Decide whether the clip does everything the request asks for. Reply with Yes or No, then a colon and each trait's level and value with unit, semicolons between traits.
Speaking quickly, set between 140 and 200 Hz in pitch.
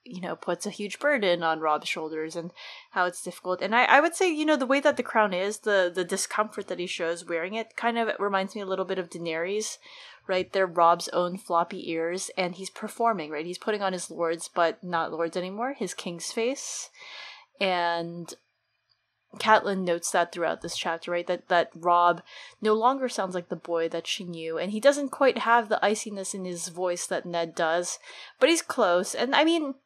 Yes: fast, 210 wpm; medium, 185 Hz